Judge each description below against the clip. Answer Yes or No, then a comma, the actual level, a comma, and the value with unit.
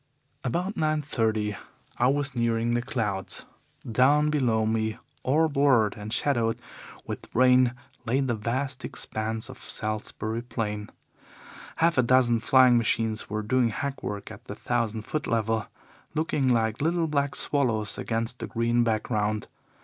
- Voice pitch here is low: Yes, low, 120 Hz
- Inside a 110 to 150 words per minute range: Yes, average, 140 wpm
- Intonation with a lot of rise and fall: No, average, 3.5 semitones